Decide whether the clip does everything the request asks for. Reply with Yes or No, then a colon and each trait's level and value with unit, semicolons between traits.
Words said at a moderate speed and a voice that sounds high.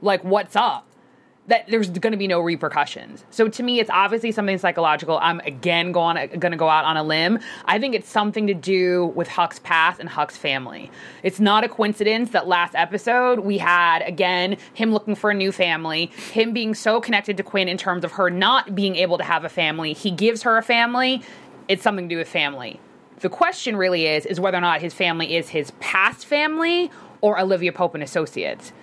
No: fast, 210 wpm; high, 195 Hz